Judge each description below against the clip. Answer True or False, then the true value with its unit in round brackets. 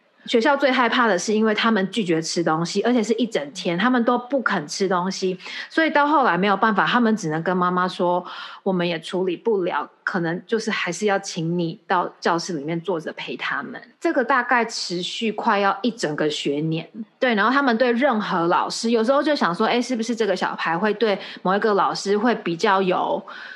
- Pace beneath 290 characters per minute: False (310 characters per minute)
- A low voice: False (210 Hz)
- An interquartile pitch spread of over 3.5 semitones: True (5.2 semitones)